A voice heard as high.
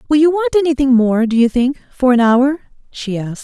Yes: very high, 260 Hz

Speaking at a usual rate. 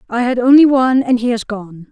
No: fast, 250 wpm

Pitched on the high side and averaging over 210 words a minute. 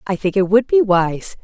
Yes: high, 205 Hz; fast, 250 wpm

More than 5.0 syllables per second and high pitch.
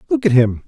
No: 6.5 syllables/s; medium, 140 Hz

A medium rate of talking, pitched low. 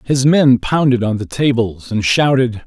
Yes: average, 180 wpm; low, 125 Hz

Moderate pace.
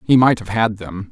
No: fast, 270 wpm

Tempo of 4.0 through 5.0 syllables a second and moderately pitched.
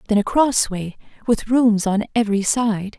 No: 4.6 syllables/s; high, 215 Hz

